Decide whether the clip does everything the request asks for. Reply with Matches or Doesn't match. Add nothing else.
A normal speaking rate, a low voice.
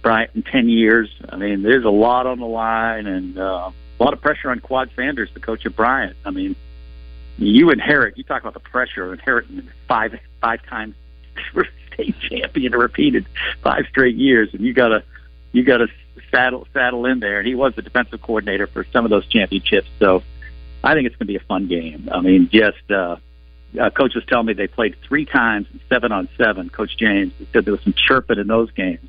Doesn't match